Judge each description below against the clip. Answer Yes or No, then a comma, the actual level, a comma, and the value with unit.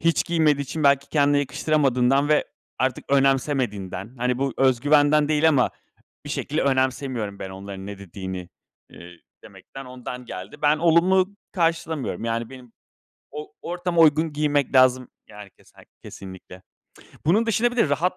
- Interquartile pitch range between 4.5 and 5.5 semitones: No, average, 4.0 semitones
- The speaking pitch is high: No, medium, 140 Hz